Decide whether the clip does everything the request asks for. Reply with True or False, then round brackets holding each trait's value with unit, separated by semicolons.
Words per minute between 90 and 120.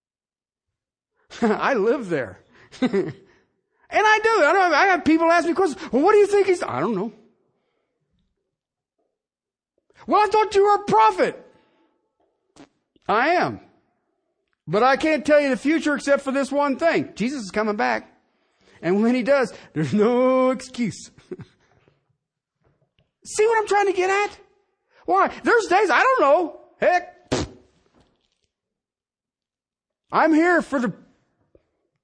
False (140 wpm)